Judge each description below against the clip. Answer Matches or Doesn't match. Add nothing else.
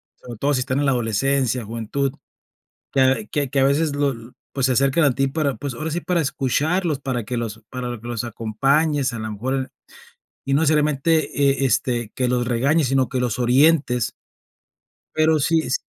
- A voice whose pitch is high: Doesn't match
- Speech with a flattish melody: Doesn't match